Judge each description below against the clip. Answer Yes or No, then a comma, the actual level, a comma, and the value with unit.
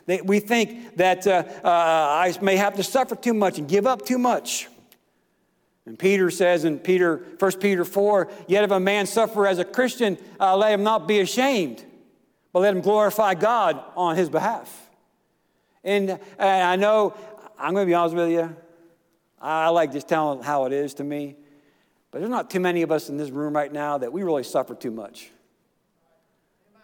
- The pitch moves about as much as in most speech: Yes, average, 3.5 semitones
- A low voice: No, medium, 185 Hz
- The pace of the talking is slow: No, average, 190 wpm